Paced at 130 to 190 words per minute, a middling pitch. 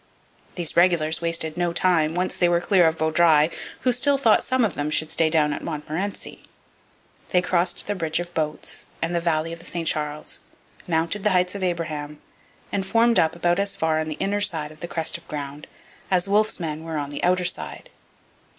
No: fast, 205 wpm; medium, 170 Hz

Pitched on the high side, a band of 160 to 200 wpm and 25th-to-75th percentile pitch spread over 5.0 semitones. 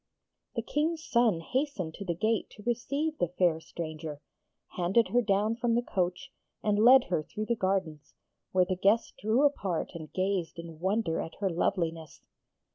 Yes: high, 195 Hz; average, 170 wpm; wide, 5.6 semitones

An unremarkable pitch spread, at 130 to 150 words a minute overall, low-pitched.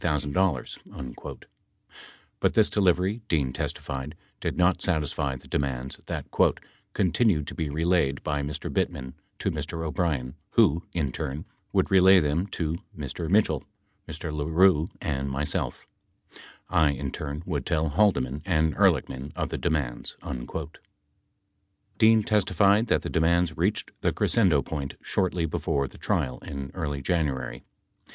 Yes: average, 4.4 semitones; slow, 135 wpm; very low, 80 Hz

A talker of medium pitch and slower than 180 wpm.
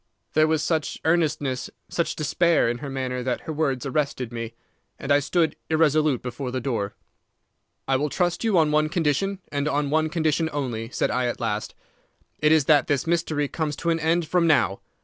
No: medium, 150 Hz; average, 190 wpm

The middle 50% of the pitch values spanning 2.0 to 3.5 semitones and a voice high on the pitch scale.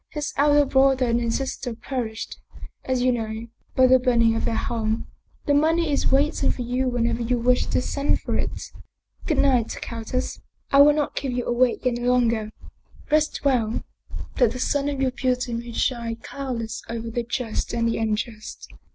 Yes: average, 2.7 semitones; very high, 250 Hz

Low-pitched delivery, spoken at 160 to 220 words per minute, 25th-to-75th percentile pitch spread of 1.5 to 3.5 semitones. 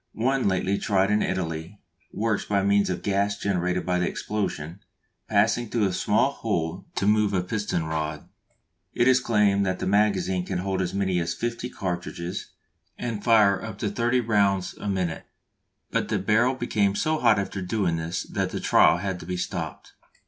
Yes: low, 100 Hz; average, 180 wpm; average, 2.8 semitones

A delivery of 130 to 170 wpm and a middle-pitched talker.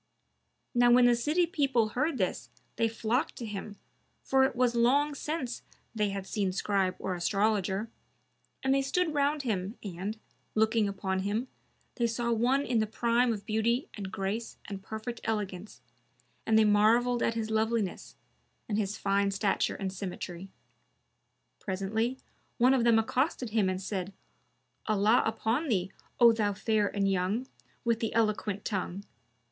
No: average, 155 wpm; high, 220 Hz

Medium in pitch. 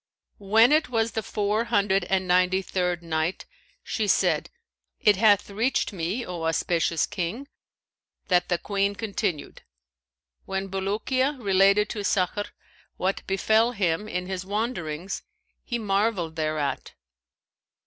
No: high, 195 Hz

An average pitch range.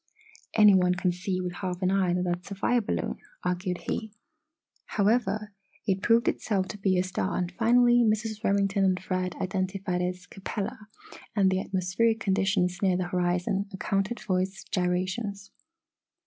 No: narrow, 2.2 semitones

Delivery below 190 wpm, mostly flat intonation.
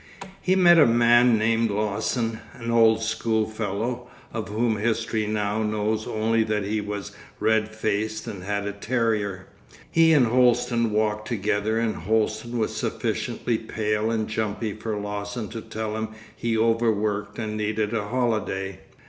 Yes: average, 150 wpm; narrow, 1.5 semitones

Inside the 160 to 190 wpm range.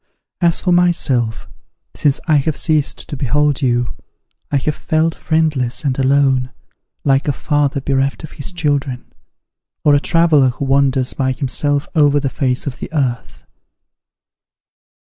No: average, 140 wpm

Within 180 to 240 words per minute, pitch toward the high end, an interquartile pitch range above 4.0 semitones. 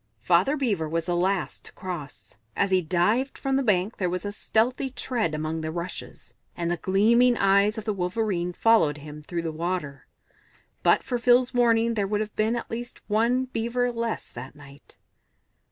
Yes: average, 185 wpm; high, 200 Hz; average, 5.3 semitones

